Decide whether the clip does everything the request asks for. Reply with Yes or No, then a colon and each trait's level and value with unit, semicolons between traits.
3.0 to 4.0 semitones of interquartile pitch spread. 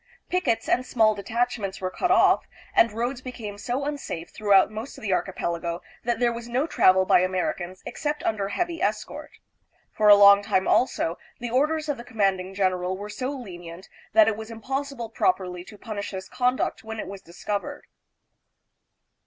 No: average, 4.8 semitones